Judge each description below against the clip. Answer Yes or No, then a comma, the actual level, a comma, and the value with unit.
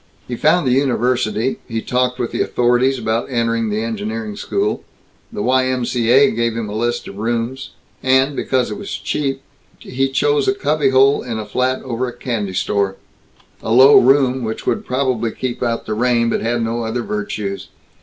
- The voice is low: Yes, low, 120 Hz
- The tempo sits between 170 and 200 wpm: Yes, average, 185 wpm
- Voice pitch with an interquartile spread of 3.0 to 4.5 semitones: No, narrow, 2.5 semitones